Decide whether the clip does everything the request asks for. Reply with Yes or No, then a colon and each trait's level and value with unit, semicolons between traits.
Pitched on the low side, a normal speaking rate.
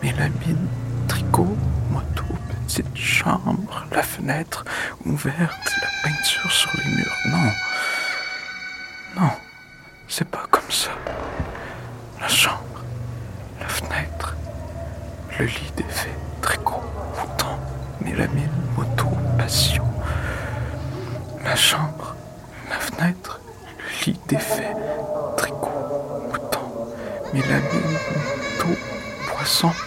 No: low, 125 Hz; slow, 90 wpm